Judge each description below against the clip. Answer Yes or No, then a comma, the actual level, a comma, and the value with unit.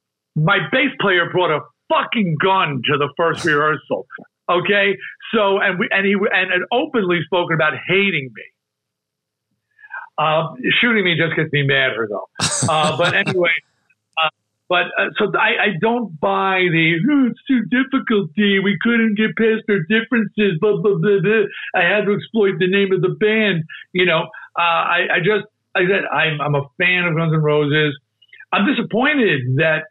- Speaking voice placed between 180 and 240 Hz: Yes, high, 190 Hz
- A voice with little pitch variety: No, average, 4.9 semitones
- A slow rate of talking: No, average, 170 wpm